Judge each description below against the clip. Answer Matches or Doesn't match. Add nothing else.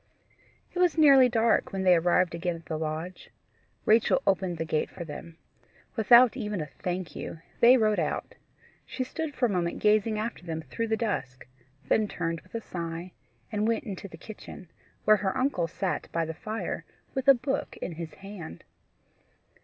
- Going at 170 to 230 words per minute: Matches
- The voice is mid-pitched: Doesn't match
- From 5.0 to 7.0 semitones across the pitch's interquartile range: Matches